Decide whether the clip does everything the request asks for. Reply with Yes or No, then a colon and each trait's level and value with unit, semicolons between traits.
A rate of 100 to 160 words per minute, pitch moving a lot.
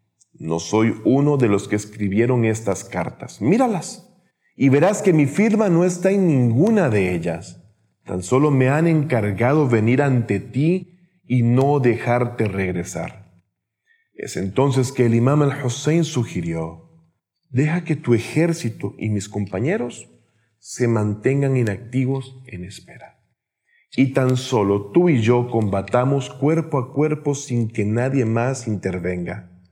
Yes: average, 135 wpm; wide, 6.0 semitones